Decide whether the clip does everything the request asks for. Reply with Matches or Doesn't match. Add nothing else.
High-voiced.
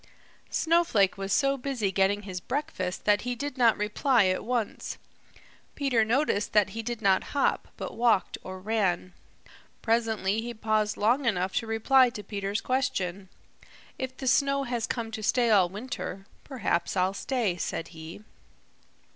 Matches